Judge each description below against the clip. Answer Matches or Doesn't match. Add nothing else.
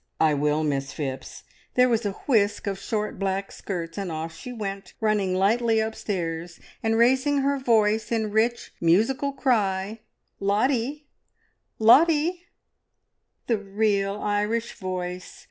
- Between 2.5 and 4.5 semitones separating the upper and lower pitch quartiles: Matches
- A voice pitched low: Doesn't match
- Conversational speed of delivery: Doesn't match